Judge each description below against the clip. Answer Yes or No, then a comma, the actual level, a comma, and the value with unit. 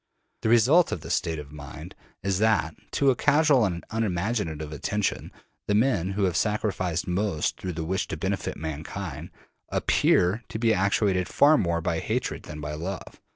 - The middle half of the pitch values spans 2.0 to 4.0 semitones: No, average, 5.1 semitones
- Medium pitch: No, very low, 95 Hz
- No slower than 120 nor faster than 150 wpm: No, average, 170 wpm